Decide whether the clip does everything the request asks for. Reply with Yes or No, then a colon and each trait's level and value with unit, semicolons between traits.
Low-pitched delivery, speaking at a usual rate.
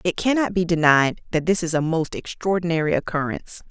No: medium, 170 Hz; average, 180 wpm